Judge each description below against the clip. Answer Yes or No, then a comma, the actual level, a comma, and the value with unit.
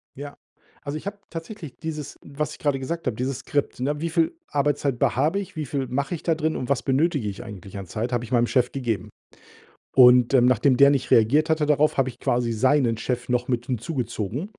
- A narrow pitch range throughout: No, average, 3.7 semitones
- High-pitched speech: No, low, 135 Hz